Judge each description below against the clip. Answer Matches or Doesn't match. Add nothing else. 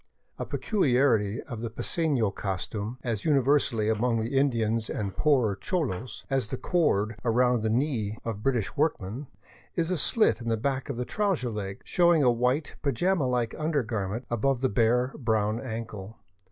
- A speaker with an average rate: Matches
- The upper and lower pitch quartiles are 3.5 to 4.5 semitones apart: Matches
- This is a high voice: Doesn't match